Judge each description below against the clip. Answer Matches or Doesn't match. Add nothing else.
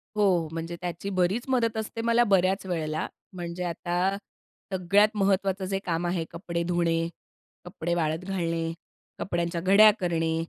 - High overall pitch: Doesn't match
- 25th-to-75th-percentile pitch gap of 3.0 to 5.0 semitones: Doesn't match